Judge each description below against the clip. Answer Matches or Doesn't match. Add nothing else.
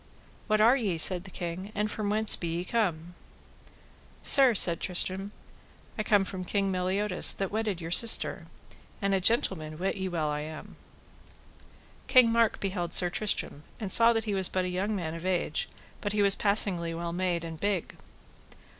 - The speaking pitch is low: Doesn't match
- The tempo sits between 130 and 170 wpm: Doesn't match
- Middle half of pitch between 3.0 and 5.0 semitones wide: Matches